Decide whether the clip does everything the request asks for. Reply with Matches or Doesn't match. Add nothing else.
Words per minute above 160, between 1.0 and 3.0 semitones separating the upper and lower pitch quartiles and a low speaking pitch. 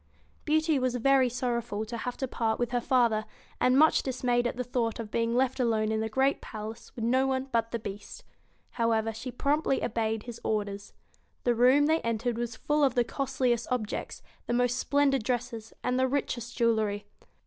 Doesn't match